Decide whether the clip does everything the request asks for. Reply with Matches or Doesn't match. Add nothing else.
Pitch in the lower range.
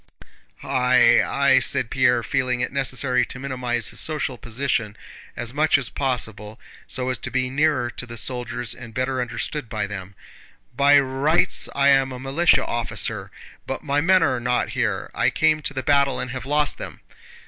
Matches